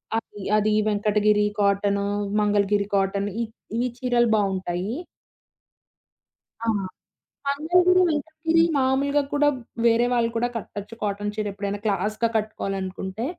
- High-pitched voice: Yes, high, 210 Hz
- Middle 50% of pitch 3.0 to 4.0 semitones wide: Yes, average, 3.5 semitones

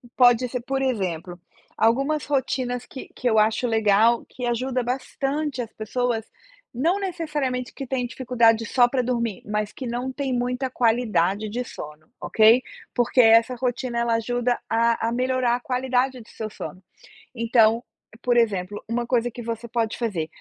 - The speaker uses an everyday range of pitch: No, narrow, 2.1 semitones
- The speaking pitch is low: No, high, 240 Hz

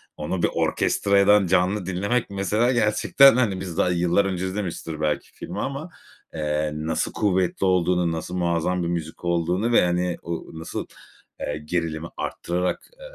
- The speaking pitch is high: No, very low, 90 Hz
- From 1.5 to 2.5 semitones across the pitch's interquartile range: No, average, 2.9 semitones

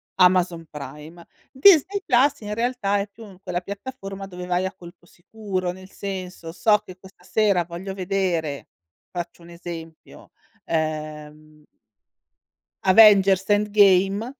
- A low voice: No, medium, 185 Hz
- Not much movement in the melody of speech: No, average, 3.0 semitones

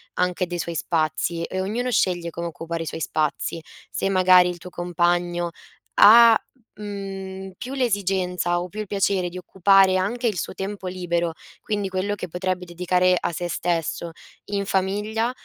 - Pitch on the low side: No, medium, 185 Hz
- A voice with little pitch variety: Yes, narrow, 2.3 semitones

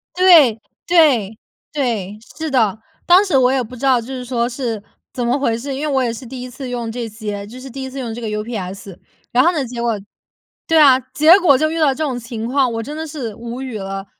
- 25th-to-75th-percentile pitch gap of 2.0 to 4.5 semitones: Yes, average, 3.5 semitones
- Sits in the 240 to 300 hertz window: Yes, very high, 250 Hz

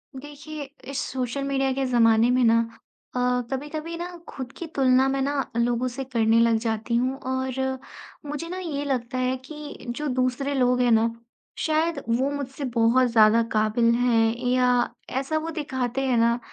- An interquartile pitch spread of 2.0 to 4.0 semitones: Yes, average, 2.9 semitones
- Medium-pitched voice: No, very high, 255 Hz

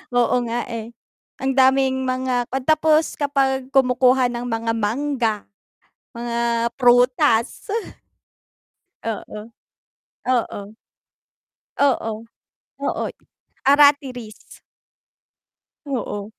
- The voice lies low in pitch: No, very high, 250 Hz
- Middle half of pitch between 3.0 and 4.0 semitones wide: No, narrow, 2.4 semitones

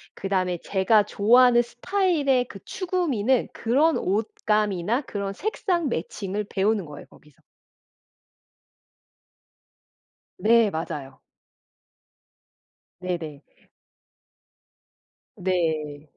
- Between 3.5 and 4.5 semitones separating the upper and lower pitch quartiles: No, wide, 5.5 semitones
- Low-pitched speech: No, high, 205 Hz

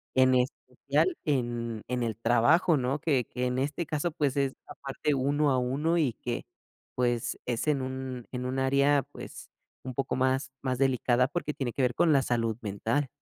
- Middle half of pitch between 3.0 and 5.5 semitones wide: No, narrow, 2.5 semitones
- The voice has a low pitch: Yes, low, 130 Hz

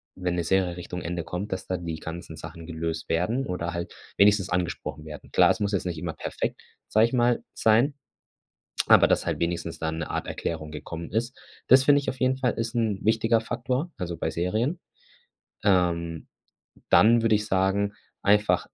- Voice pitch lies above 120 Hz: No, very low, 95 Hz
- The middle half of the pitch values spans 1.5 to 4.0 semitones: No, average, 5.1 semitones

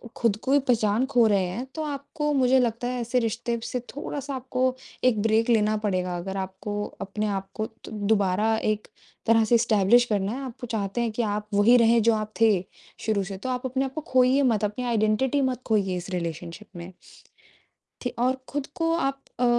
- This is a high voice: Yes, high, 225 Hz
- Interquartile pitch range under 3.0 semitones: No, average, 3.7 semitones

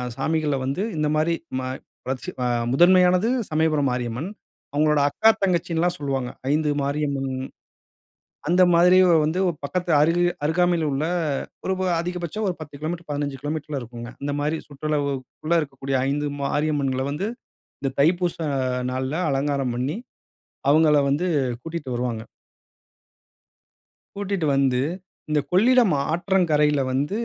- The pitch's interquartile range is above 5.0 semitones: No, average, 4.0 semitones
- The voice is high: No, medium, 150 Hz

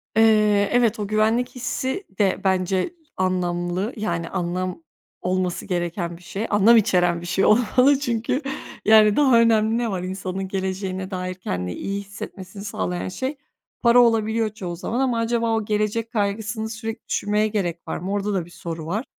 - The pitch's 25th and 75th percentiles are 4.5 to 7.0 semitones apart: No, average, 3.5 semitones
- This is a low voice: No, high, 205 Hz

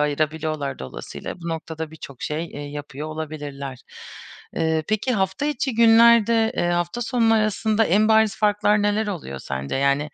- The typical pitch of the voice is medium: Yes, medium, 175 Hz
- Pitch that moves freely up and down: Yes, wide, 6.6 semitones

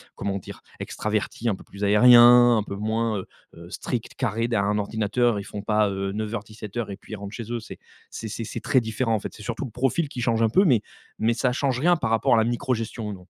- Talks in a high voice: No, low, 110 Hz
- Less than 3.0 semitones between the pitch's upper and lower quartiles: Yes, narrow, 2.5 semitones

